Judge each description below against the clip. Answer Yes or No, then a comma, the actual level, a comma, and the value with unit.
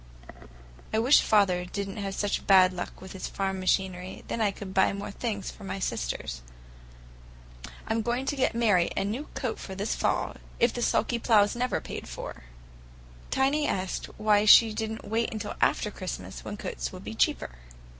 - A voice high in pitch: Yes, high, 205 Hz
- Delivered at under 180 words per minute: No, average, 185 wpm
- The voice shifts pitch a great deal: No, average, 3.1 semitones